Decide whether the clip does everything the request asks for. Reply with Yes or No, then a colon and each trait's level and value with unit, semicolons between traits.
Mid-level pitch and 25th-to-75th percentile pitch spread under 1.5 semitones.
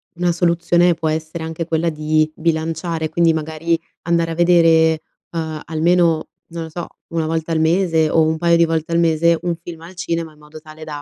Yes: medium, 165 Hz; narrow, 1.1 semitones